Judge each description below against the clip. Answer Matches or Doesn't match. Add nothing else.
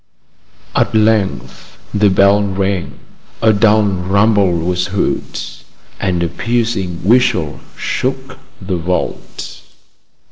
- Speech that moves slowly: Matches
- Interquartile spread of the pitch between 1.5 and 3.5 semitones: Matches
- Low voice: Matches